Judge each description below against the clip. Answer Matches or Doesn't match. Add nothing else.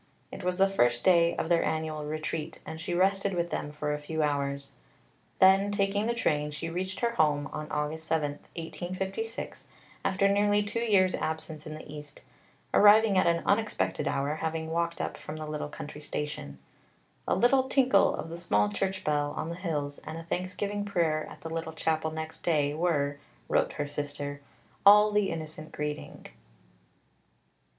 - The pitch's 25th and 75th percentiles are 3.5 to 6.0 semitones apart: Matches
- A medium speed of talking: Matches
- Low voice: Doesn't match